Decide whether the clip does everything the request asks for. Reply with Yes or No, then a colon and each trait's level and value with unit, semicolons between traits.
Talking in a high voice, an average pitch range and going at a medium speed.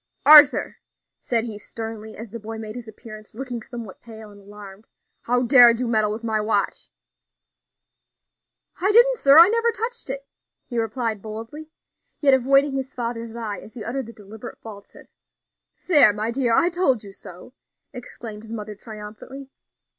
Yes: high, 230 Hz; average, 3.7 semitones; average, 160 wpm